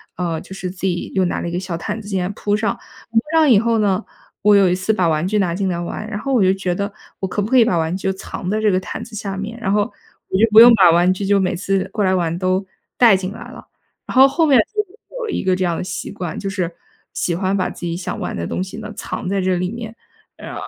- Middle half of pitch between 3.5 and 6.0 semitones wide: No, average, 2.8 semitones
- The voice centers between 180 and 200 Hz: Yes, high, 195 Hz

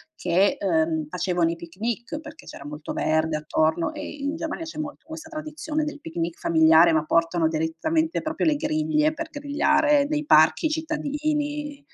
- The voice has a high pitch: Yes, very high, 285 Hz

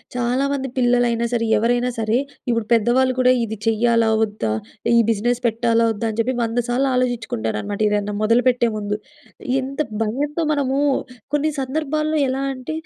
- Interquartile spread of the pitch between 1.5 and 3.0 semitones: Yes, narrow, 2.6 semitones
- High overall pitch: Yes, high, 240 Hz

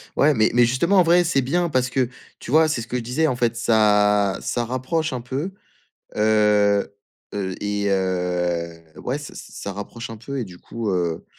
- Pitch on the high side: No, low, 115 Hz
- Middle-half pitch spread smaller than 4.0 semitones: No, average, 4.6 semitones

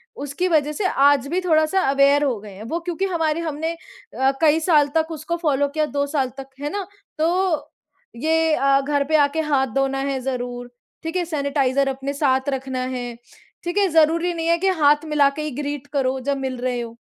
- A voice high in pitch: Yes, very high, 290 Hz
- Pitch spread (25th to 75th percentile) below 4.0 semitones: Yes, average, 3.2 semitones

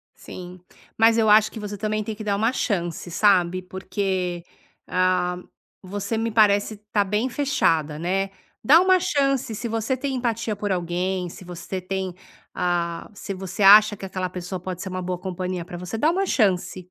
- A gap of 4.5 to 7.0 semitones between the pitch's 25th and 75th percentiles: No, average, 3.3 semitones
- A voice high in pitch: Yes, high, 195 Hz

